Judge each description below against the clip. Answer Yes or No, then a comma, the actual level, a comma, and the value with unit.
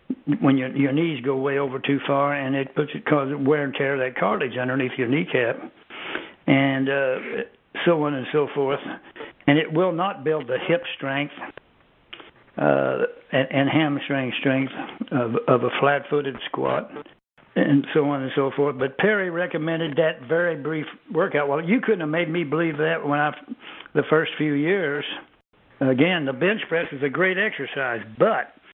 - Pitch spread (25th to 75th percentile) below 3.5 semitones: Yes, average, 3.1 semitones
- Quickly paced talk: No, average, 175 wpm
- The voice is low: No, medium, 145 Hz